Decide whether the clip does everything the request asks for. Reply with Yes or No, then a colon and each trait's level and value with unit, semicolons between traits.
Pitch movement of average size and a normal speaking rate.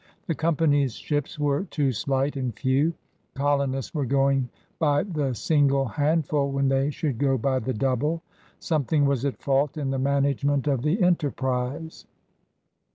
No: narrow, 1.8 semitones; average, 160 wpm